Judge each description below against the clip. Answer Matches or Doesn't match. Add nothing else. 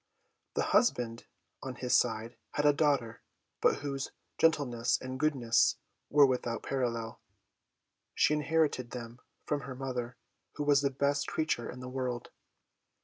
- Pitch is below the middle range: Matches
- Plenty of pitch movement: Doesn't match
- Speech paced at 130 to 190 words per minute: Matches